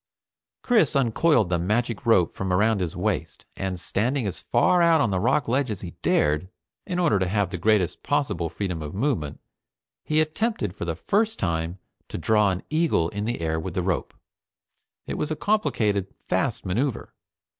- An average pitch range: No, wide, 8.1 semitones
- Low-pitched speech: Yes, low, 105 Hz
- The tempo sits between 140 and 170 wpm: No, average, 180 wpm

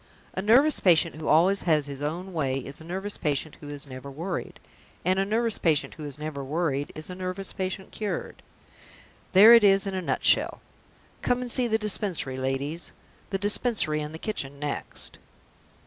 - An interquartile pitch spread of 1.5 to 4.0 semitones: No, average, 5.2 semitones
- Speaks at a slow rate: No, average, 180 wpm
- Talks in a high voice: No, medium, 170 Hz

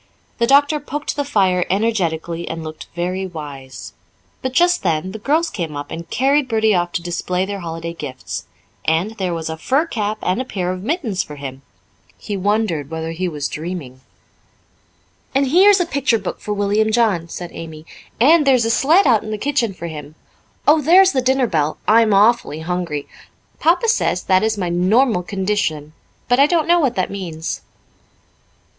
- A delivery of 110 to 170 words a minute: No, average, 185 wpm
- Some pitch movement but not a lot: No, wide, 7.6 semitones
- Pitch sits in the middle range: No, high, 195 Hz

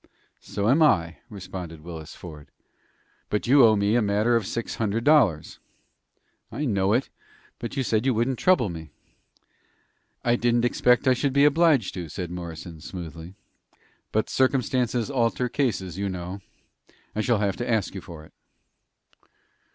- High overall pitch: No, low, 110 Hz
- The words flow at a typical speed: Yes, average, 155 wpm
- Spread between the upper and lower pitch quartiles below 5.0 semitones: No, wide, 5.5 semitones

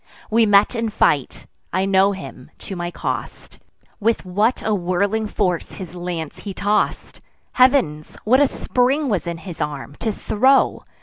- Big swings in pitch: No, average, 4.3 semitones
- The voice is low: No, high, 200 Hz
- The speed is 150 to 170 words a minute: Yes, average, 160 wpm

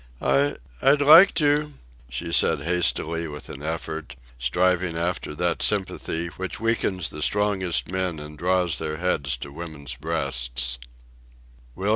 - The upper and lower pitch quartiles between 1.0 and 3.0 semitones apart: No, average, 4.0 semitones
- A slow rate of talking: Yes, slow, 130 wpm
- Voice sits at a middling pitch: No, very low, 85 Hz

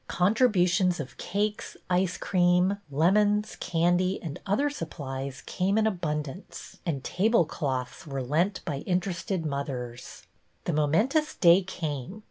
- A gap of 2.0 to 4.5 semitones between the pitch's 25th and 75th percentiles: No, average, 5.2 semitones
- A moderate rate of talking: No, slow, 125 wpm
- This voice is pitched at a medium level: Yes, medium, 175 Hz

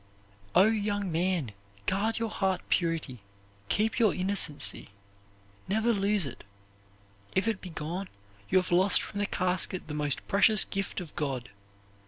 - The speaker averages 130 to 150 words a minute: Yes, average, 140 wpm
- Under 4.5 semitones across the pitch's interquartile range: Yes, average, 3.8 semitones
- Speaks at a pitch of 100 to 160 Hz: No, high, 190 Hz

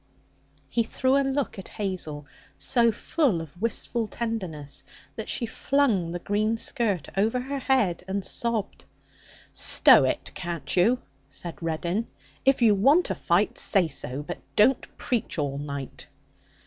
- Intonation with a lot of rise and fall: Yes, wide, 5.9 semitones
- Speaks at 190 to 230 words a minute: No, average, 145 wpm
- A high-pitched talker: Yes, high, 205 Hz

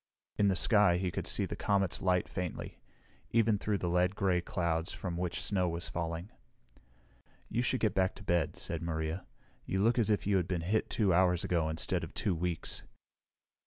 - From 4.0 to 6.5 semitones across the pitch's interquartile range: No, average, 2.8 semitones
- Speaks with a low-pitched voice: Yes, very low, 90 Hz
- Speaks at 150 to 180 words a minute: No, average, 195 wpm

